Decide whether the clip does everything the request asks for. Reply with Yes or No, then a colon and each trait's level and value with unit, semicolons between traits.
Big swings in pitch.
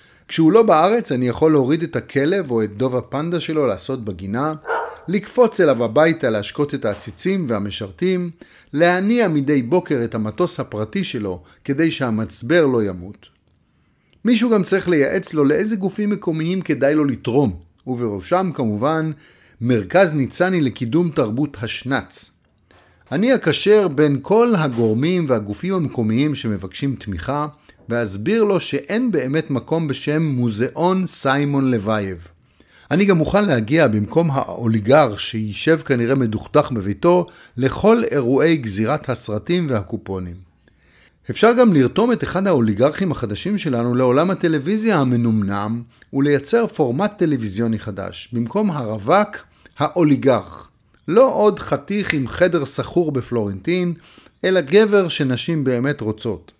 Yes: wide, 7.6 semitones